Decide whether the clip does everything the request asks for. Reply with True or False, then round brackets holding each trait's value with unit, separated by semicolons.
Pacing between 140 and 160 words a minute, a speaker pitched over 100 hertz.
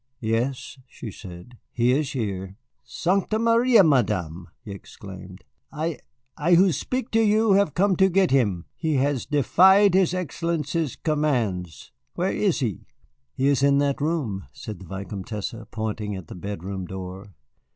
True (150 wpm; 135 Hz)